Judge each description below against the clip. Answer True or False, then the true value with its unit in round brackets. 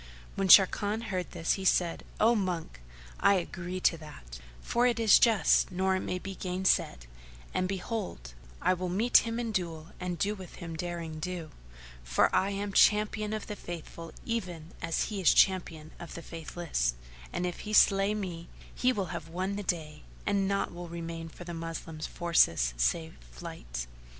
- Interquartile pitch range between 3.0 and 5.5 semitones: True (3.3 semitones)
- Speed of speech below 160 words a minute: False (175 wpm)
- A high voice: False (180 Hz)